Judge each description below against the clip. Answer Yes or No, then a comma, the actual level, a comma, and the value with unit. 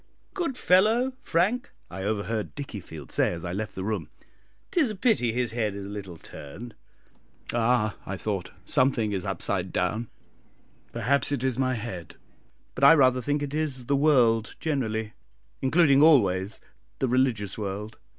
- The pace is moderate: Yes, average, 160 wpm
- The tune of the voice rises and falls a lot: Yes, wide, 5.8 semitones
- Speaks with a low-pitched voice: Yes, low, 120 Hz